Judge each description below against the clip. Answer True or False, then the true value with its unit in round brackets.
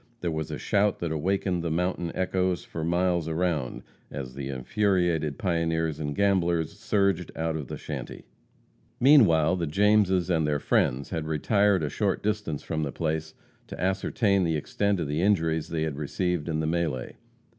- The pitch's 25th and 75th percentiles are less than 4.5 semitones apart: True (3.2 semitones)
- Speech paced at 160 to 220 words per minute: True (170 wpm)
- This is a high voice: False (85 Hz)